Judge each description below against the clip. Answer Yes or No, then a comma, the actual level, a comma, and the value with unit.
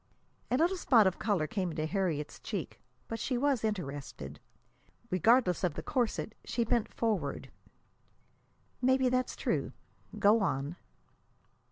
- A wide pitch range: Yes, wide, 7.3 semitones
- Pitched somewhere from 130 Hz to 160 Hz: No, high, 210 Hz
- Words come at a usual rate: No, slow, 130 wpm